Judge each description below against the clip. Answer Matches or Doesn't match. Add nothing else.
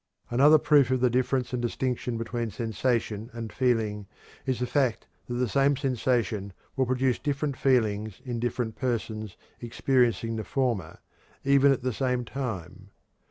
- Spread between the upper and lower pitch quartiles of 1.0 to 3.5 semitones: Matches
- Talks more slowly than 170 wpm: Matches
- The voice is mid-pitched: Doesn't match